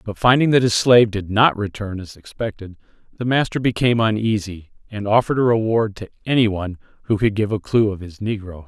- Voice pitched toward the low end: Yes, low, 105 Hz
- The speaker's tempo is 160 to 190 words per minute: No, average, 200 wpm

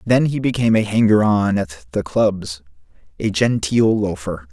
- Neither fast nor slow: Yes, average, 160 wpm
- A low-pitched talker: Yes, low, 105 Hz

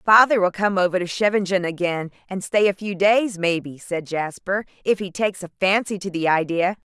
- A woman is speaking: Yes, female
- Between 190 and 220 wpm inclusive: Yes, average, 200 wpm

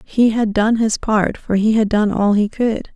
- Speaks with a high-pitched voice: Yes, high, 215 Hz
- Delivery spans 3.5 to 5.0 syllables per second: Yes, 4.4 syllables/s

